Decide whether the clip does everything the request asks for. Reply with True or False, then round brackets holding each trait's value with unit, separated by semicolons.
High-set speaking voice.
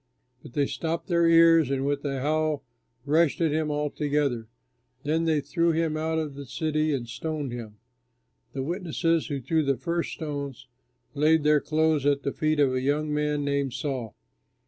False (150 Hz)